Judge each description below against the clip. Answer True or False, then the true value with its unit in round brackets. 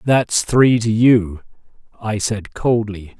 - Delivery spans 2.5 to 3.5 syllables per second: True (3.2 syllables/s)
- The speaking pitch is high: False (110 Hz)